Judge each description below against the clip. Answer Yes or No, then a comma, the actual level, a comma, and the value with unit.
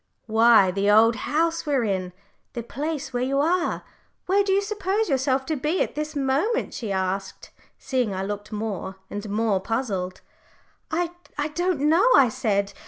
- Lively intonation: Yes, wide, 7.4 semitones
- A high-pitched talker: Yes, very high, 255 Hz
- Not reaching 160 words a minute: No, average, 165 wpm